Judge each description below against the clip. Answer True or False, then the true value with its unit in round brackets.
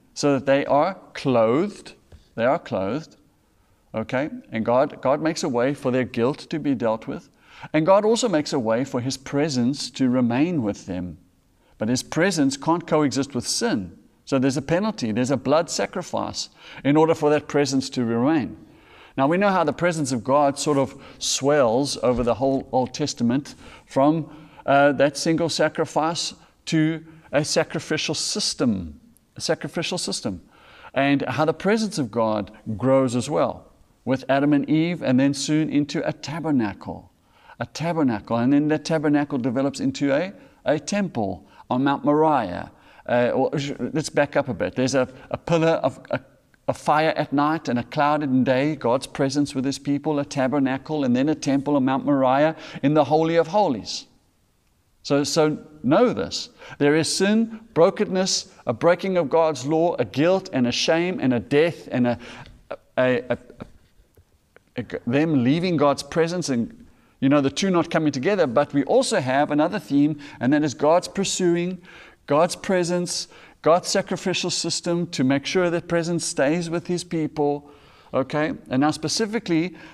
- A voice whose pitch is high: False (150 Hz)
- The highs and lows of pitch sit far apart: False (3.6 semitones)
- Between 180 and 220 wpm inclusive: False (170 wpm)